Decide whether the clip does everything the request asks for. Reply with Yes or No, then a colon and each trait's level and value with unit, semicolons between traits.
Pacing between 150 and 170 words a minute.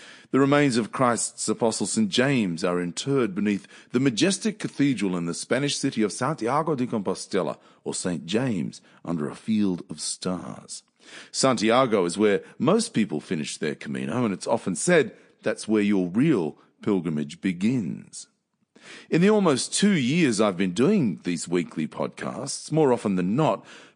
Yes: average, 155 wpm